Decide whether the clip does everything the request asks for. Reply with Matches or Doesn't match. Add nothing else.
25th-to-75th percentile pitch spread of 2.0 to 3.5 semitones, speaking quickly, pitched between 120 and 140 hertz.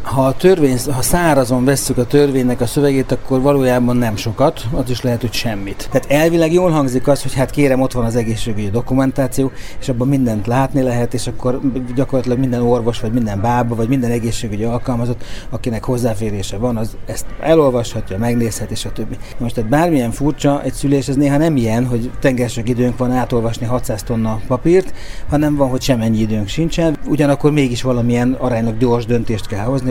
Matches